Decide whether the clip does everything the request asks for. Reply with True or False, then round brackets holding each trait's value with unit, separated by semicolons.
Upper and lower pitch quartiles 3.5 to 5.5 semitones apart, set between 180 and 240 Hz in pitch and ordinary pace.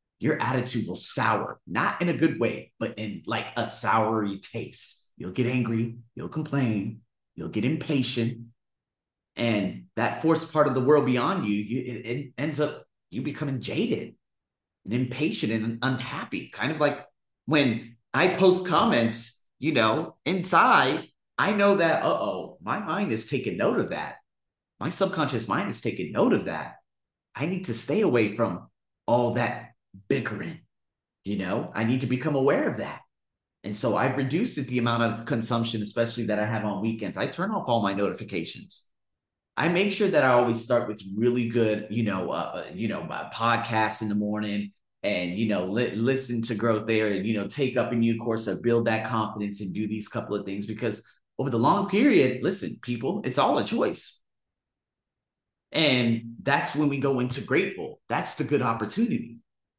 False (4.0 semitones; 115 Hz; 185 wpm)